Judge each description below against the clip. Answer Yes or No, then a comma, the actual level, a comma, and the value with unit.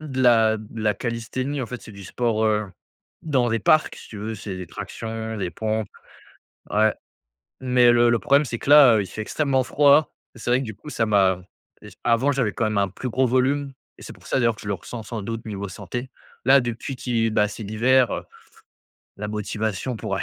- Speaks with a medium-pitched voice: No, low, 115 Hz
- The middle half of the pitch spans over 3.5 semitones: No, average, 3.2 semitones